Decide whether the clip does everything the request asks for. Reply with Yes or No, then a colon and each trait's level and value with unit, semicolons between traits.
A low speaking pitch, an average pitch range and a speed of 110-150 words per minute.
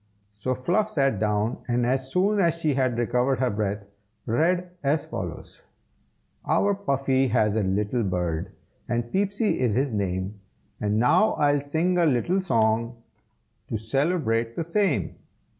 No: low, 130 Hz; wide, 7.1 semitones; average, 145 wpm